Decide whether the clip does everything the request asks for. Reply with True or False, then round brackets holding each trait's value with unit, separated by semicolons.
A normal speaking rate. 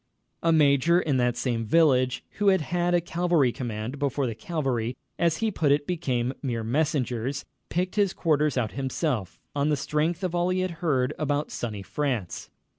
True (180 wpm)